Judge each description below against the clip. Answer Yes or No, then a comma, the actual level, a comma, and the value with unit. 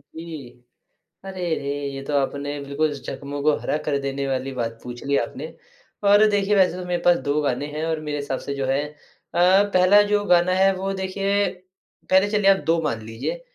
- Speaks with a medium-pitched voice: Yes, medium, 155 Hz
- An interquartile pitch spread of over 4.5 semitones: Yes, average, 5.3 semitones